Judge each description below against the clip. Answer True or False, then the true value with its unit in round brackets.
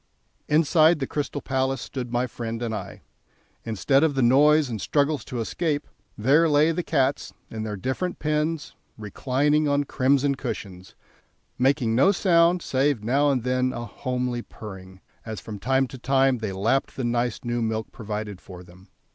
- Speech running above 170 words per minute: False (165 wpm)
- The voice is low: True (130 Hz)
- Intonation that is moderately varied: True (4.4 semitones)